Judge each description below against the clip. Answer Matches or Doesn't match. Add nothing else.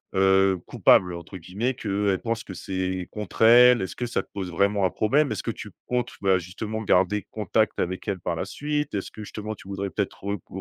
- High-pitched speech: Doesn't match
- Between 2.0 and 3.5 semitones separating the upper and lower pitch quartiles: Matches